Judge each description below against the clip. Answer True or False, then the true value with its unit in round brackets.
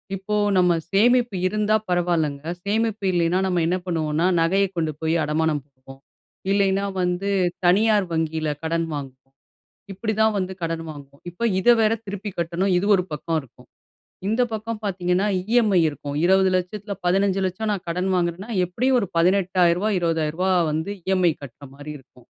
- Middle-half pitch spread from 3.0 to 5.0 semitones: True (3.7 semitones)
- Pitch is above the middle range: False (180 Hz)